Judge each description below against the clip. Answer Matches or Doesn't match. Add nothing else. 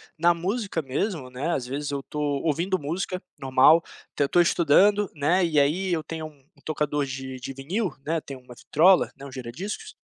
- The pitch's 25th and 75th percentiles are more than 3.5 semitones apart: Matches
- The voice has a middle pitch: Matches